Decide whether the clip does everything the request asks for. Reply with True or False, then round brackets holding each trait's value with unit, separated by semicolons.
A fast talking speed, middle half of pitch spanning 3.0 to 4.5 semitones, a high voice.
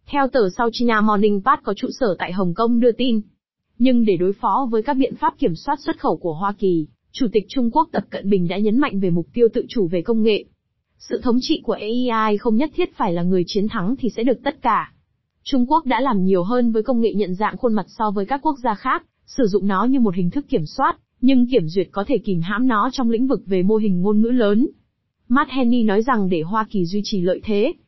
True (260 wpm; 4.2 semitones; 225 Hz)